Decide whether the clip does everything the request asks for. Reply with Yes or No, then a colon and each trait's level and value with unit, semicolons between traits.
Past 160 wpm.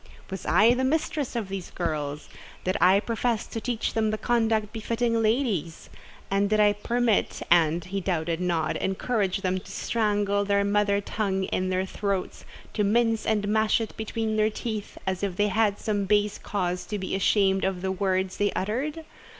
Yes: average, 175 wpm